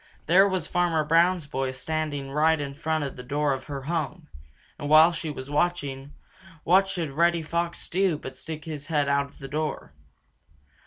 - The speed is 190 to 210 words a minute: No, average, 175 wpm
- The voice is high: No, medium, 155 Hz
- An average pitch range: Yes, average, 3.2 semitones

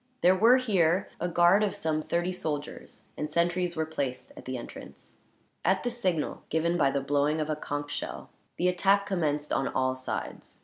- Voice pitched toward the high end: No, medium, 165 Hz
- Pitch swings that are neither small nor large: Yes, average, 3.8 semitones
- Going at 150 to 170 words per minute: No, average, 185 wpm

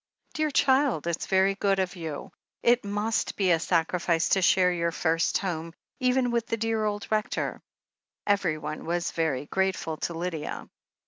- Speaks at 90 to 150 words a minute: No, average, 170 wpm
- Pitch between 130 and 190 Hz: Yes, medium, 185 Hz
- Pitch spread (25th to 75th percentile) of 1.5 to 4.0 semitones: No, average, 4.4 semitones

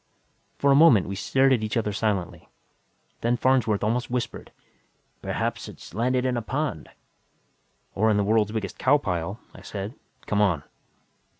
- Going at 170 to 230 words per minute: No, average, 160 wpm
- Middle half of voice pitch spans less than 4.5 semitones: Yes, average, 3.9 semitones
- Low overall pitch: Yes, low, 110 Hz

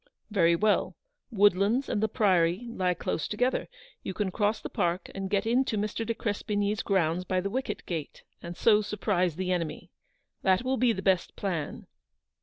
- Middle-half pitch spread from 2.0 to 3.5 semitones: Yes, average, 3.1 semitones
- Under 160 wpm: No, average, 175 wpm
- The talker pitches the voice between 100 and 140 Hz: No, high, 200 Hz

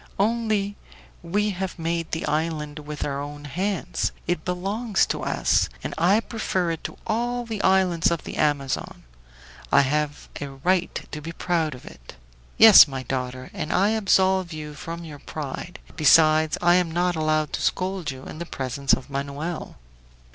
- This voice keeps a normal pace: Yes, average, 170 wpm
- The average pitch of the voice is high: No, medium, 165 Hz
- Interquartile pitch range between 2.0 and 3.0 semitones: No, average, 4.3 semitones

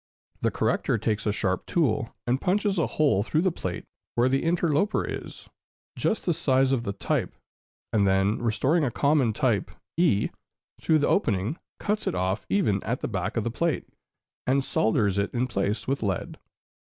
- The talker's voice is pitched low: Yes, low, 120 Hz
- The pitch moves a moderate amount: No, wide, 7.1 semitones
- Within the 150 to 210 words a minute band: Yes, average, 180 wpm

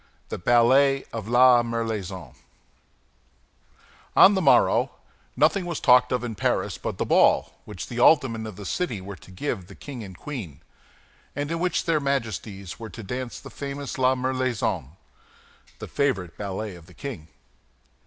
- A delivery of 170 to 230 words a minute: No, average, 160 wpm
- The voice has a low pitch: Yes, low, 120 Hz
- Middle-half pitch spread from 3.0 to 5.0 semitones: No, wide, 5.5 semitones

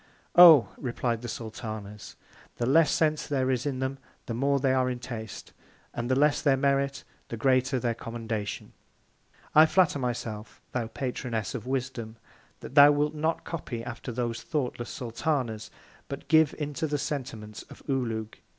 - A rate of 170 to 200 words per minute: No, average, 160 wpm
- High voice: No, low, 130 Hz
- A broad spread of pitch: No, average, 3.5 semitones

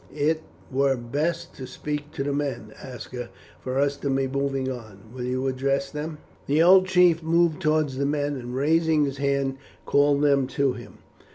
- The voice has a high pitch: No, medium, 140 Hz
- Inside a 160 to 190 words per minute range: Yes, average, 180 wpm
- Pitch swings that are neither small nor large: No, narrow, 2.3 semitones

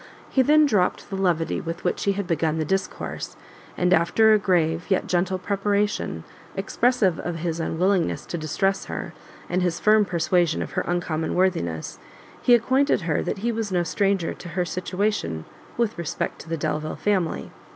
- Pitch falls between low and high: Yes, medium, 180 Hz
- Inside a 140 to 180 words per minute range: Yes, average, 170 wpm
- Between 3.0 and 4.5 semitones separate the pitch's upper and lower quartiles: Yes, average, 3.6 semitones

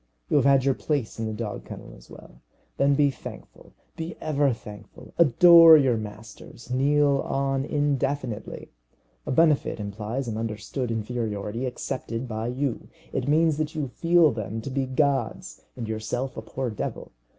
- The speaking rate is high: No, average, 160 wpm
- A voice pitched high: No, low, 130 Hz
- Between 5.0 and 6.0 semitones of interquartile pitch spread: No, average, 4.3 semitones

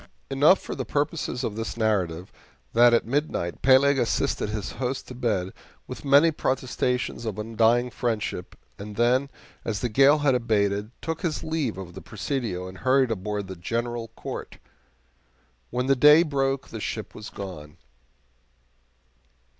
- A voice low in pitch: Yes, low, 120 Hz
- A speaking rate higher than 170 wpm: No, average, 150 wpm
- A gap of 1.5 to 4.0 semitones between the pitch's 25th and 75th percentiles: No, average, 4.5 semitones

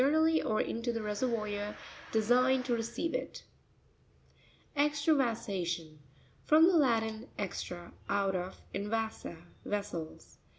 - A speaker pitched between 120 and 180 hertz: No, high, 220 Hz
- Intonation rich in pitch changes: No, average, 4.4 semitones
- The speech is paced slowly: Yes, slow, 100 wpm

